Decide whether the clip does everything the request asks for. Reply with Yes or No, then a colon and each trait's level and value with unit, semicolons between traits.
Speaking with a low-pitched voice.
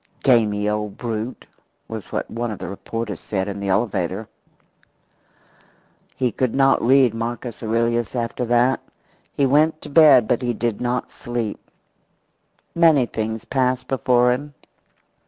Yes: low, 120 Hz